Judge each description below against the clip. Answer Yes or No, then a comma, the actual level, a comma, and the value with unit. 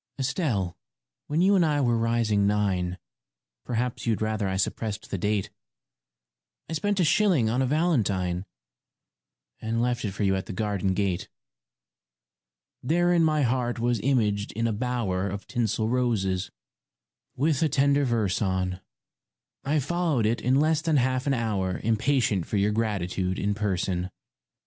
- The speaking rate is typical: Yes, average, 155 wpm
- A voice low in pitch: Yes, low, 115 Hz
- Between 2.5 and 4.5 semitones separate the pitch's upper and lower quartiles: No, average, 5.3 semitones